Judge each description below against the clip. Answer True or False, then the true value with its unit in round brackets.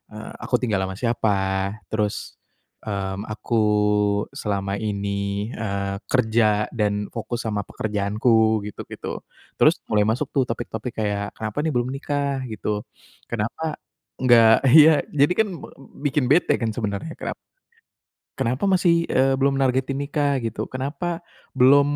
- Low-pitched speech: True (115 Hz)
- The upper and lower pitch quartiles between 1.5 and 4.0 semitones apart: False (4.7 semitones)